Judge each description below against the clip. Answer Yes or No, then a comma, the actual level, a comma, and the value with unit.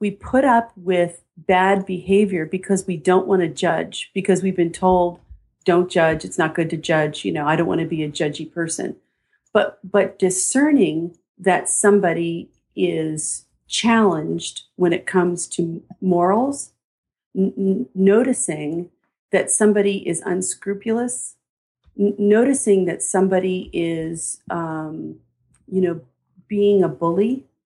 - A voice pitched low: No, medium, 185 Hz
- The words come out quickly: No, slow, 135 wpm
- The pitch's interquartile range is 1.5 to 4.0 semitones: Yes, average, 3.0 semitones